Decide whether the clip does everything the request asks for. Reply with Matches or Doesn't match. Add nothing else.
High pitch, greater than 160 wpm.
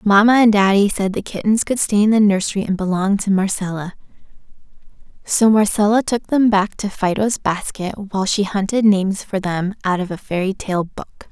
Matches